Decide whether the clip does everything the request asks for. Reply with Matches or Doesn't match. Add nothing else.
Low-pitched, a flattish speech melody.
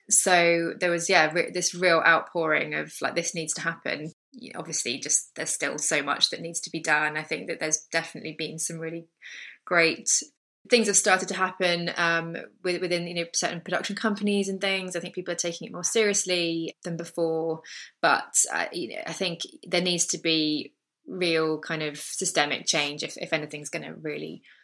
Doesn't match